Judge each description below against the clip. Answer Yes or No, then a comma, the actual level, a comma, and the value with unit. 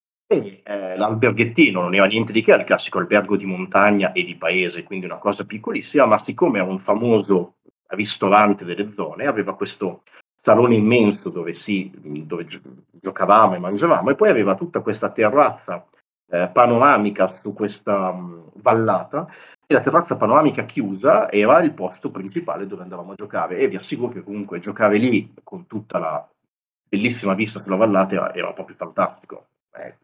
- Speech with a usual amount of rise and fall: No, narrow, 2.3 semitones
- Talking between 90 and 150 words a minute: No, average, 165 wpm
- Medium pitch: No, low, 100 Hz